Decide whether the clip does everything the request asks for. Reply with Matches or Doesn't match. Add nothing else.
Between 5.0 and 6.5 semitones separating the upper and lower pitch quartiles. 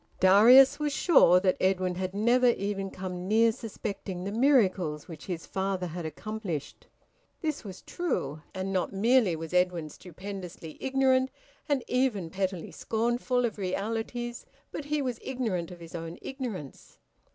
Matches